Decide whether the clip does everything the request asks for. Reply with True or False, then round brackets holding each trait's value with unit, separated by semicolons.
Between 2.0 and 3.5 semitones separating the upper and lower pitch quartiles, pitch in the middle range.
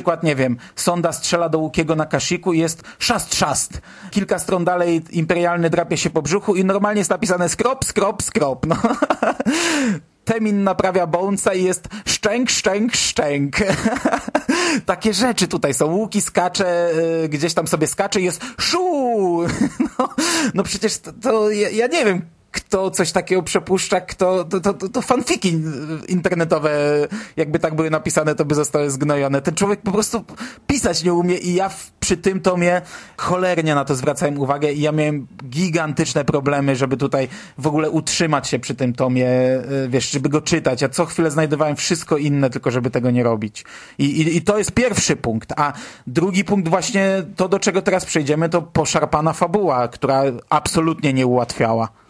False (4.6 semitones; 175 Hz)